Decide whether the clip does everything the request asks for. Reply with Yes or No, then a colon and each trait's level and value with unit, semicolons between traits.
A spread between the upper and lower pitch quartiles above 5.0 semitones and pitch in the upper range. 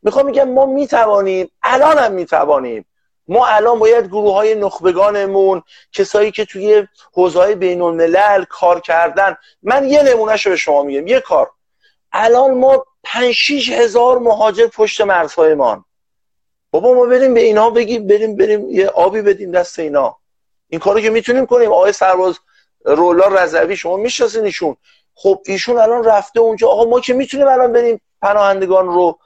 Yes: wide, 5.4 semitones; high, 220 Hz